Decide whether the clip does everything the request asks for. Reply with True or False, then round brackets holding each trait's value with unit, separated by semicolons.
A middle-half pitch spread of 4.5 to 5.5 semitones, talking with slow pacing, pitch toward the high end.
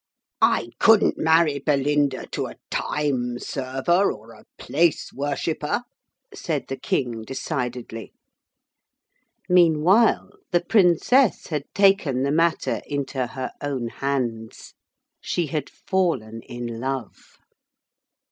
False (4.9 semitones; 105 wpm; 140 Hz)